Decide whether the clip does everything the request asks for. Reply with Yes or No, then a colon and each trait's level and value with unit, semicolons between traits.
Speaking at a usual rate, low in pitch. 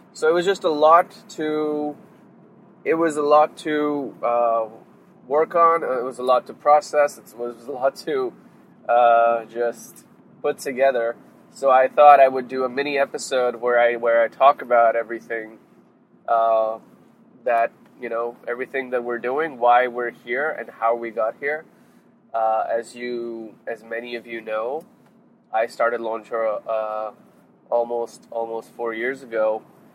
Yes: average, 160 wpm; low, 120 Hz